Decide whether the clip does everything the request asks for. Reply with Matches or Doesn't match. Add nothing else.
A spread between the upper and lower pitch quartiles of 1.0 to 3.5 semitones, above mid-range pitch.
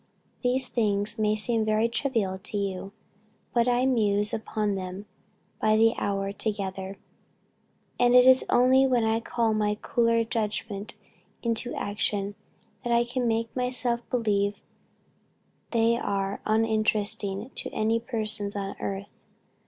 Matches